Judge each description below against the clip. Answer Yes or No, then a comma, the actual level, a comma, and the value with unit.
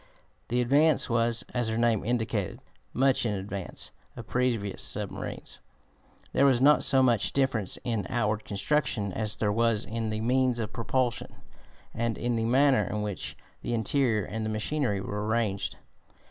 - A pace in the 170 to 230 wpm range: No, average, 160 wpm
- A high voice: No, low, 115 Hz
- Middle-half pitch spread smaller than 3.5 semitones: Yes, average, 2.8 semitones